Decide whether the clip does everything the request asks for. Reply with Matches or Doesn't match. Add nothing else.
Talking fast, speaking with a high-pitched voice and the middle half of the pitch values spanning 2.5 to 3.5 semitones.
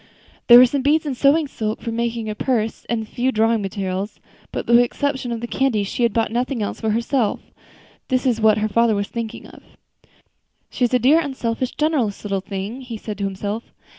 Matches